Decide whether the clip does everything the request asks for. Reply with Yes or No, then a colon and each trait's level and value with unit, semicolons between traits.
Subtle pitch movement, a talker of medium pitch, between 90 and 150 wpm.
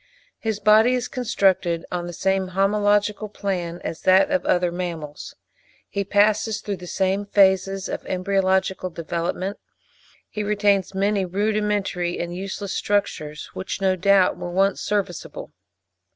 No: narrow, 2.2 semitones; high, 195 Hz; slow, 135 wpm